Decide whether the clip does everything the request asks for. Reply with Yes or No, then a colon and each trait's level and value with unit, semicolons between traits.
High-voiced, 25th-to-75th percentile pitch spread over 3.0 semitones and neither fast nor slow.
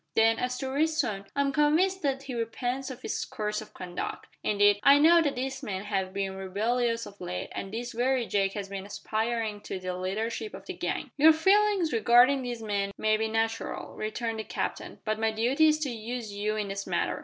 No: high, 225 Hz; average, 4.5 semitones; fast, 210 wpm